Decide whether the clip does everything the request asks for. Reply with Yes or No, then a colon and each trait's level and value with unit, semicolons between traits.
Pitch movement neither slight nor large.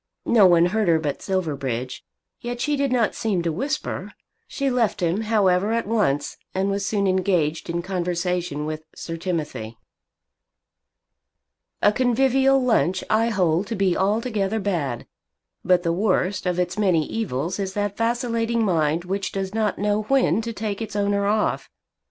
Yes: average, 4.3 semitones